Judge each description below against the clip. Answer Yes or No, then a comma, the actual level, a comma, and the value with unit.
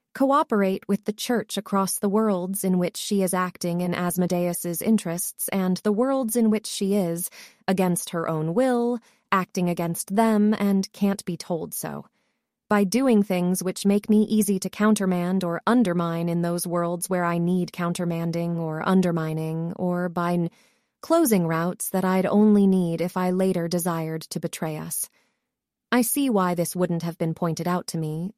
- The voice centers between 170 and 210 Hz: Yes, medium, 185 Hz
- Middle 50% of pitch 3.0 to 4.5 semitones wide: Yes, average, 3.3 semitones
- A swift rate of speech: No, average, 170 wpm